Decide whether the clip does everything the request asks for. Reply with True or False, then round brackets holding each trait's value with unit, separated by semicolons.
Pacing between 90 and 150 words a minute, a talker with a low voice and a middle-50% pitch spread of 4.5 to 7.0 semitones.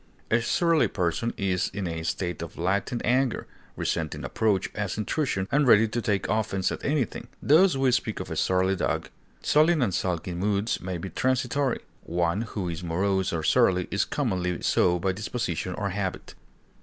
False (170 wpm; 100 Hz; 4.8 semitones)